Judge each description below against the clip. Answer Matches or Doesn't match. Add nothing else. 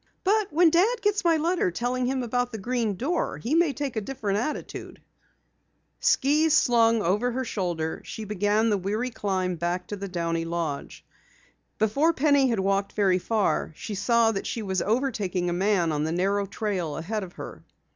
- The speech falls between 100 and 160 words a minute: Doesn't match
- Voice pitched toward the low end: Doesn't match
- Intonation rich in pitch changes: Matches